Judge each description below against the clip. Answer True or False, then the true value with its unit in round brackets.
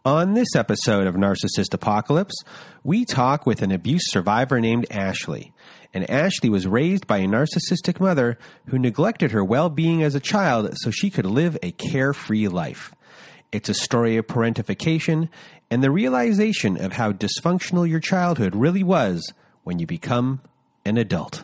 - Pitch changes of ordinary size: False (7.8 semitones)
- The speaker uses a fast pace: False (155 wpm)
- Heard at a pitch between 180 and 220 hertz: False (145 Hz)